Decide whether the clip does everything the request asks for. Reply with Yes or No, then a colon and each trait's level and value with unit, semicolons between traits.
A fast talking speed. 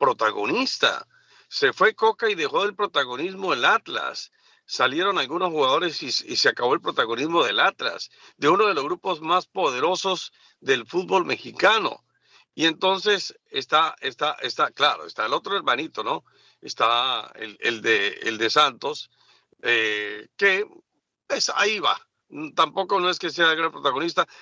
No: average, 150 wpm